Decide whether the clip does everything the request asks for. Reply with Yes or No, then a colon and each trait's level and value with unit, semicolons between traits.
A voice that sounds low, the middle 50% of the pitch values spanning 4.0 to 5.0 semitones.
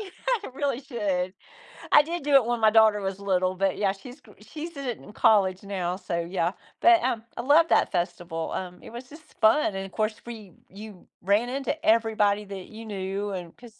No: high, 210 Hz; average, 4.5 semitones